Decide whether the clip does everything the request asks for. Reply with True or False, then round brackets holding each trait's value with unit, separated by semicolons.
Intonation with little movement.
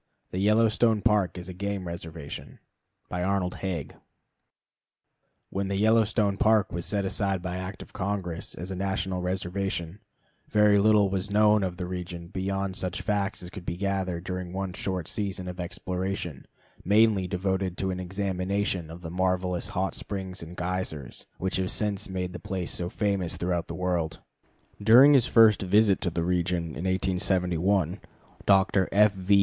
True (2.0 semitones)